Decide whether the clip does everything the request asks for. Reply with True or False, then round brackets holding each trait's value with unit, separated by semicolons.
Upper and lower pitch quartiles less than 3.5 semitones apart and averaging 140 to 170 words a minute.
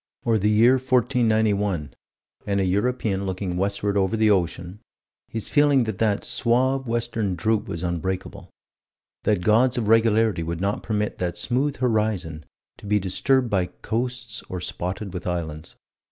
False (3.9 semitones; 150 wpm)